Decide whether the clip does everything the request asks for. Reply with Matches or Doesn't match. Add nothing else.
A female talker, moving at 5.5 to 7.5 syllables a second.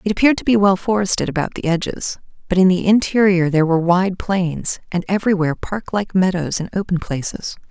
Matches